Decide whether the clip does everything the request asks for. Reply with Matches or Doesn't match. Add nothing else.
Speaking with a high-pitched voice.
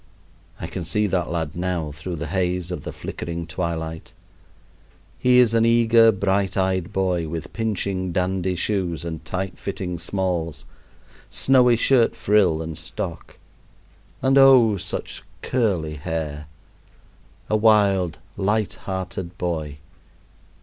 Doesn't match